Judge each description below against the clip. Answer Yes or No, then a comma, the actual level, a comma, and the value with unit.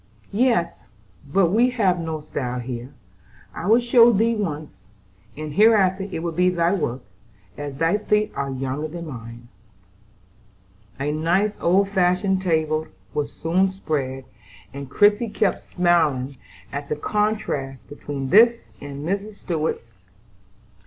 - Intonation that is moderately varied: No, wide, 5.9 semitones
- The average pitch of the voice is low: No, medium, 170 Hz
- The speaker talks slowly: Yes, slow, 130 wpm